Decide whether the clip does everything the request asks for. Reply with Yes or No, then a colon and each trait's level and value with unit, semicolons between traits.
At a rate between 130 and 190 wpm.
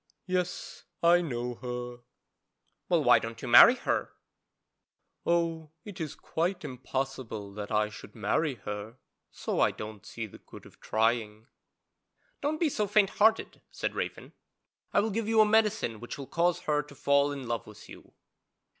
Yes: average, 165 wpm